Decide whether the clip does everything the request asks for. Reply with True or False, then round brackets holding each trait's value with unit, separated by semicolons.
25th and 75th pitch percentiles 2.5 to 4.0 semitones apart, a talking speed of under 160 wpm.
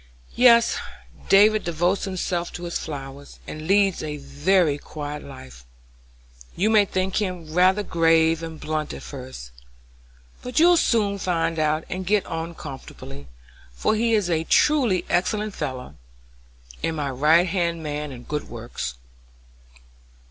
False (4.6 semitones; 140 wpm)